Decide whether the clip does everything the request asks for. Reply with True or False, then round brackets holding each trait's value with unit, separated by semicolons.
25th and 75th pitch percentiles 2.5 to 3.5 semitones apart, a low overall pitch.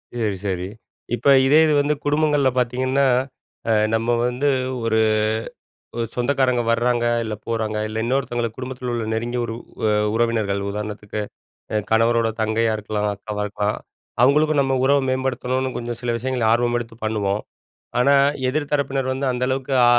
True (2.9 semitones; 120 Hz)